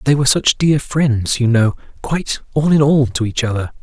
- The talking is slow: No, fast, 205 wpm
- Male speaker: Yes, male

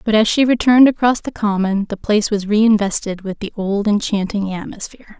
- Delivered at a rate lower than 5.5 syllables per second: No, 5.6 syllables/s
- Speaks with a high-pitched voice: Yes, high, 210 Hz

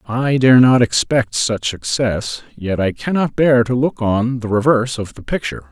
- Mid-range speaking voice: No, low, 120 Hz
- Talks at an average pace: Yes, average, 190 wpm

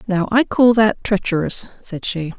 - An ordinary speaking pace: Yes, average, 175 wpm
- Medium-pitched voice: No, high, 200 Hz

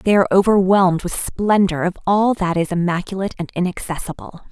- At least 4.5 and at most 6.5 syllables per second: Yes, 6.0 syllables/s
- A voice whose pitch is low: No, medium, 185 Hz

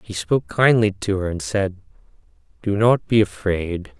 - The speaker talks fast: No, average, 165 wpm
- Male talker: Yes, male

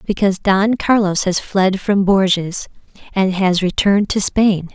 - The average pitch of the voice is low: No, high, 195 Hz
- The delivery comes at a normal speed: Yes, average, 150 wpm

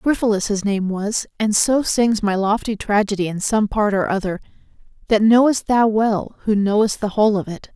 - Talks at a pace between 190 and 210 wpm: Yes, average, 195 wpm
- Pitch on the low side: No, high, 210 Hz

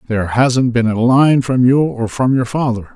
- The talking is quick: Yes, fast, 225 wpm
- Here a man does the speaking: Yes, male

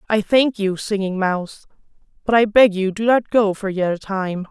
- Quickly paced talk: Yes, fast, 215 wpm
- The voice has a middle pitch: No, high, 205 Hz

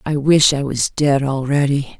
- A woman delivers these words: Yes, female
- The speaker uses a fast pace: No, average, 180 wpm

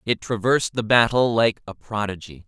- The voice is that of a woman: No, male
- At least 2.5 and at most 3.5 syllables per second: No, 5.3 syllables/s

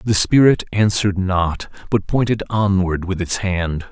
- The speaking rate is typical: Yes, average, 155 wpm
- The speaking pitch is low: Yes, very low, 95 Hz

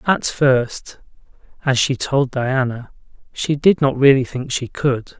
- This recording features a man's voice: Yes, male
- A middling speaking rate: Yes, average, 150 wpm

